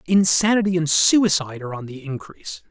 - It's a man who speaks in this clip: Yes, male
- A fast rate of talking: No, average, 155 wpm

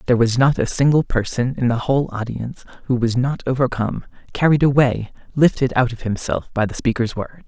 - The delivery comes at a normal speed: Yes, average, 195 wpm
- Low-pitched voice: Yes, low, 125 Hz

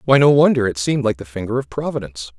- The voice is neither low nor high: No, low, 120 Hz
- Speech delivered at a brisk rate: Yes, fast, 250 wpm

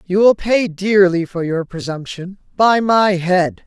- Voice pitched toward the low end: No, high, 190 Hz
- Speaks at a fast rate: No, average, 165 wpm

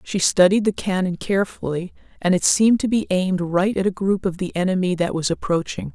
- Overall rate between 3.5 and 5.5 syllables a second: No, 5.8 syllables/s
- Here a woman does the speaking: Yes, female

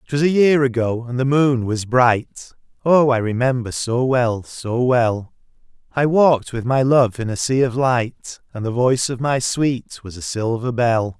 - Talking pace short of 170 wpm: No, average, 195 wpm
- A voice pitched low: Yes, low, 125 Hz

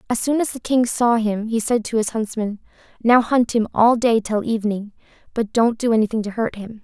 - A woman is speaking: Yes, female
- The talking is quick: Yes, fast, 230 wpm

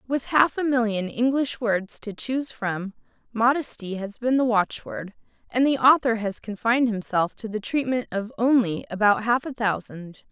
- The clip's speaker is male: No, female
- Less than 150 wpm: No, average, 170 wpm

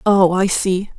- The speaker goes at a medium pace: Yes, average, 180 wpm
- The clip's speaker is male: No, female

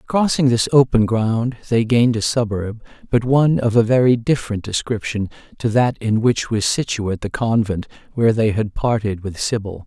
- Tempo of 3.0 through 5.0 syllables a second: No, 5.2 syllables/s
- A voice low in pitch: Yes, low, 115 Hz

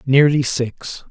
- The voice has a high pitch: No, low, 135 Hz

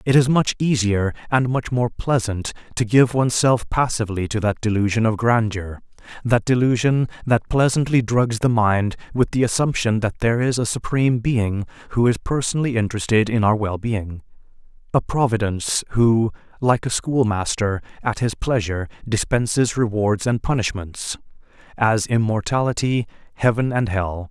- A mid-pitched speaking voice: No, low, 115 Hz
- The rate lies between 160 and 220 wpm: No, average, 145 wpm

